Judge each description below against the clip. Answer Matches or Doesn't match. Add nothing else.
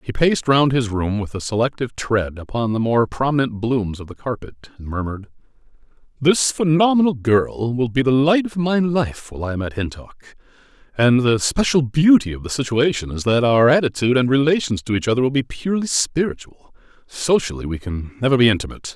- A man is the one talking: Matches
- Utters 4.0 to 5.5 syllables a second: Doesn't match